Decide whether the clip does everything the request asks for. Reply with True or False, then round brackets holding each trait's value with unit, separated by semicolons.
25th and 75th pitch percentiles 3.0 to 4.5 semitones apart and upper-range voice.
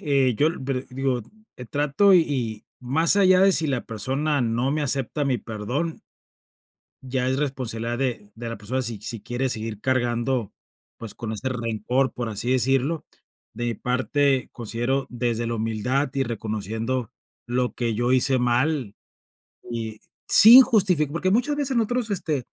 False (3.7 semitones; 130 Hz)